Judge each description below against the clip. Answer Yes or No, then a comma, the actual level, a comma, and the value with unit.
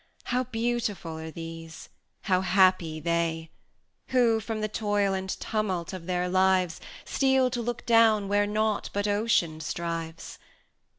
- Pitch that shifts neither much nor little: Yes, average, 4.6 semitones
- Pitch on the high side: Yes, high, 195 Hz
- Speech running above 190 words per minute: No, slow, 135 wpm